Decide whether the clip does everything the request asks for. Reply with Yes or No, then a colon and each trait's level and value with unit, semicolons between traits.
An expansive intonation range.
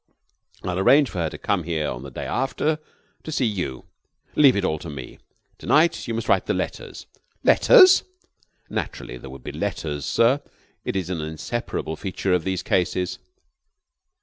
Yes: wide, 7.2 semitones